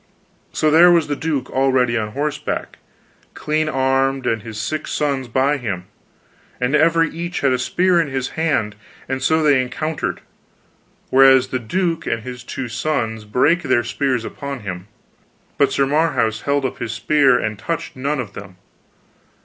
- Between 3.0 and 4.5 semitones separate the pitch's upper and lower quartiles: Yes, average, 4.2 semitones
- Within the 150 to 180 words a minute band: Yes, average, 165 wpm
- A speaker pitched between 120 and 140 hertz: Yes, low, 135 Hz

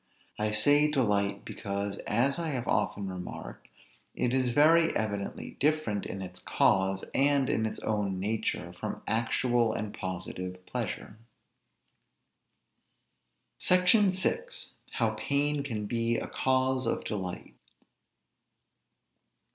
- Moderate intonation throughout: No, wide, 5.7 semitones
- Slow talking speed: Yes, slow, 115 wpm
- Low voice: Yes, low, 115 Hz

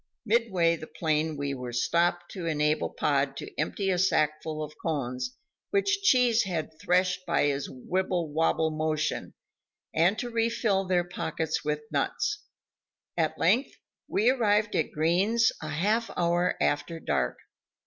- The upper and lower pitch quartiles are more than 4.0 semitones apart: Yes, average, 4.9 semitones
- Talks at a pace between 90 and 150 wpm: Yes, average, 140 wpm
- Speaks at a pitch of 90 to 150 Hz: No, medium, 170 Hz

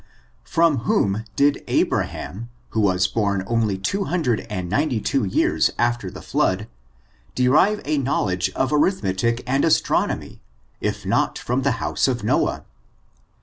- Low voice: Yes, low, 120 Hz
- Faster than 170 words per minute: No, average, 145 wpm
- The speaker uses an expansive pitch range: Yes, wide, 5.7 semitones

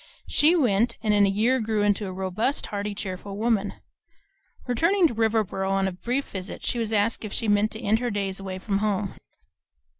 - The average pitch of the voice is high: Yes, high, 210 Hz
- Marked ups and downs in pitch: No, average, 2.7 semitones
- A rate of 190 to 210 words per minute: Yes, average, 200 wpm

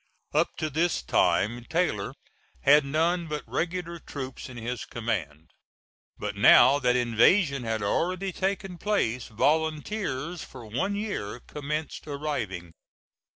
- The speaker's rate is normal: No, slow, 120 wpm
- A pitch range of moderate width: No, wide, 6.4 semitones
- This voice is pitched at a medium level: Yes, medium, 145 Hz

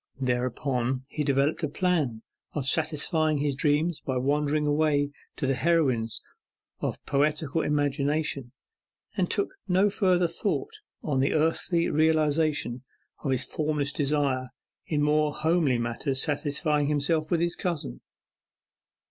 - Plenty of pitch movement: No, narrow, 2.5 semitones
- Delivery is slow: Yes, slow, 125 wpm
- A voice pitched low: No, medium, 150 Hz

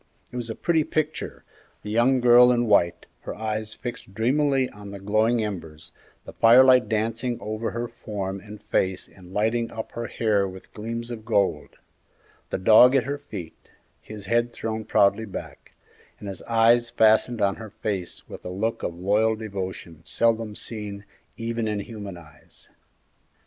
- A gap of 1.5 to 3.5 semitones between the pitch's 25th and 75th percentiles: Yes, average, 2.9 semitones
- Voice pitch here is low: Yes, low, 110 Hz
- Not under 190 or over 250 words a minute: No, average, 165 wpm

